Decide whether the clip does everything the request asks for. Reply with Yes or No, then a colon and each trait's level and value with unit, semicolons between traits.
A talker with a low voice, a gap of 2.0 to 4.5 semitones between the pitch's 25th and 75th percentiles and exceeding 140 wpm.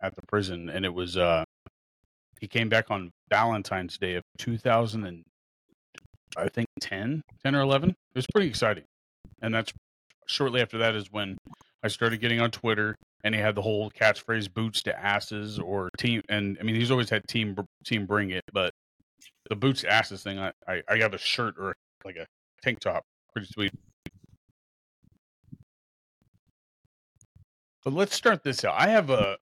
Yes: low, 105 Hz; average, 3.4 semitones; average, 175 wpm